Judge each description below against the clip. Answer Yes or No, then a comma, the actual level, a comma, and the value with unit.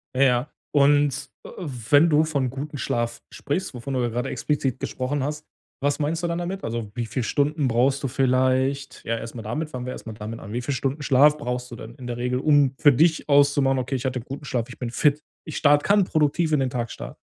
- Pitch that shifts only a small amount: No, average, 3.1 semitones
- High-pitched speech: No, low, 135 Hz